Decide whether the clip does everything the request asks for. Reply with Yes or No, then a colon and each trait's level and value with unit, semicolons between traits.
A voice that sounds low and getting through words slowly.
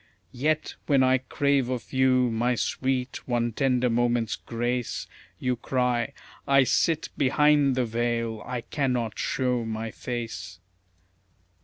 Yes: low, 125 Hz; slow, 125 wpm